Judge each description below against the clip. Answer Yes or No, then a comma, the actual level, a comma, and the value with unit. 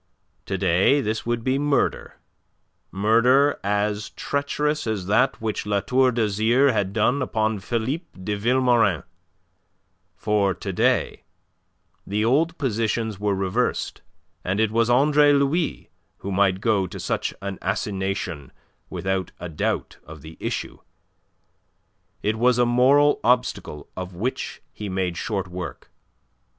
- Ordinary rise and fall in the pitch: Yes, average, 4.5 semitones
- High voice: No, low, 110 Hz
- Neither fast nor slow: No, slow, 130 wpm